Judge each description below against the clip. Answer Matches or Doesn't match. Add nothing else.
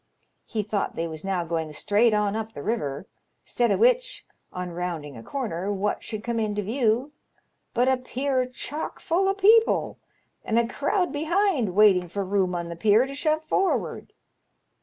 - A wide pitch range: Matches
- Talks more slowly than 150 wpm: Doesn't match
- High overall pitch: Matches